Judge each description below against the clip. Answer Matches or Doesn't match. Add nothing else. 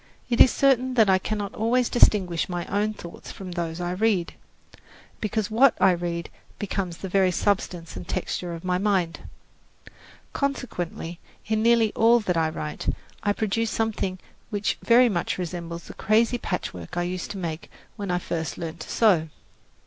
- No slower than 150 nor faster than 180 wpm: Matches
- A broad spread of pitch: Doesn't match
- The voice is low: Doesn't match